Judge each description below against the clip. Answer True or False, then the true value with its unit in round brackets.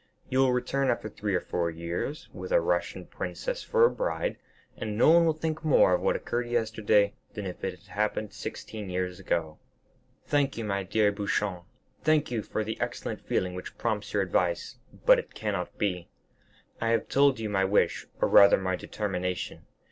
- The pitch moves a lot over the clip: True (5.7 semitones)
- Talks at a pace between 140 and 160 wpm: False (185 wpm)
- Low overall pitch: True (105 Hz)